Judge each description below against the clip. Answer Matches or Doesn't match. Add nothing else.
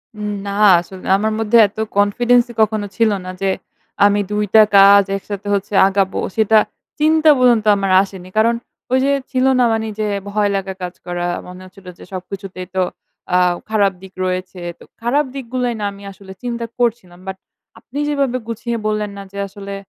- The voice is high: Matches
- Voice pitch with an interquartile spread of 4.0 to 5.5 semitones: Doesn't match